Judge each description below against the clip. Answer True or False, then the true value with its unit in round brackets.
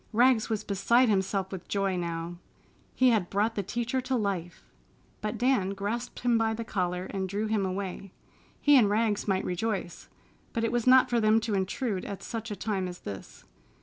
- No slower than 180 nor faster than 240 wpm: True (190 wpm)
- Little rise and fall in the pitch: False (3.3 semitones)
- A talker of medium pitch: False (210 Hz)